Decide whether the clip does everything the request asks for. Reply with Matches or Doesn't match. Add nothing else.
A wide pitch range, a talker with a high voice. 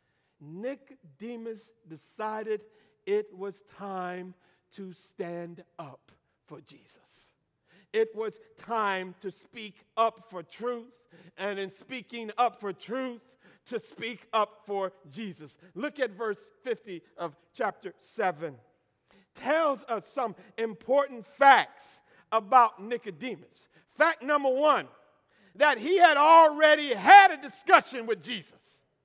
Matches